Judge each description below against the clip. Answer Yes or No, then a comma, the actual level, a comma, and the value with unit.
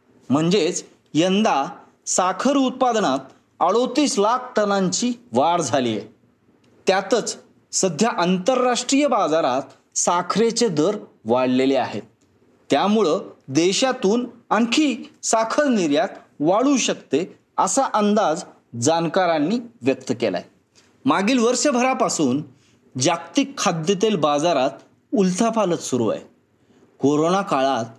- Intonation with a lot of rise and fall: Yes, wide, 8.8 semitones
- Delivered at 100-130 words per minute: No, average, 90 wpm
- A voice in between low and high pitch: No, high, 200 Hz